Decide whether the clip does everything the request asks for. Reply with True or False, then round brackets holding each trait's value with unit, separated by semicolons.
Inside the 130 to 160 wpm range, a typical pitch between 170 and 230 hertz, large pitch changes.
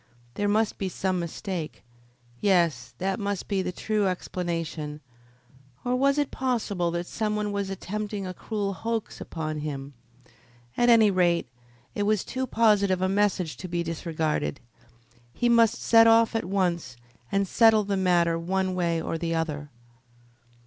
False (155 wpm; 190 Hz; 3.8 semitones)